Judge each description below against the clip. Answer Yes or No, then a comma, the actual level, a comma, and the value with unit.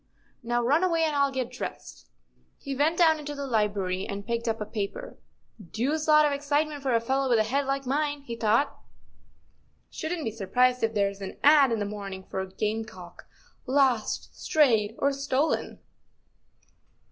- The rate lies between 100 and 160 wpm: No, average, 185 wpm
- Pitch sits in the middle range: No, very high, 250 Hz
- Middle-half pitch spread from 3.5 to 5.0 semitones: No, wide, 5.4 semitones